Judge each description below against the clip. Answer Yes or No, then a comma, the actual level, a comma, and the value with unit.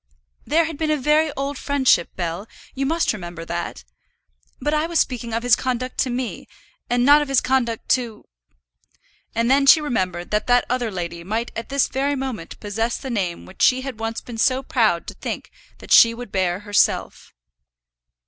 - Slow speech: No, average, 190 wpm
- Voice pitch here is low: No, high, 245 Hz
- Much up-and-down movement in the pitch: No, average, 4.5 semitones